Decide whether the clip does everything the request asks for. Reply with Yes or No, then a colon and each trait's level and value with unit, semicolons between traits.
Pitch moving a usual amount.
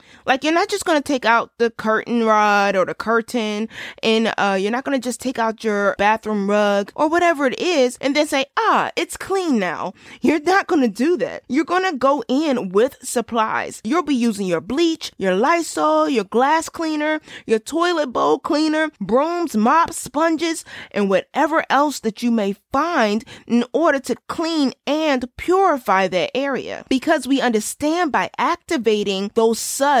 No: wide, 5.9 semitones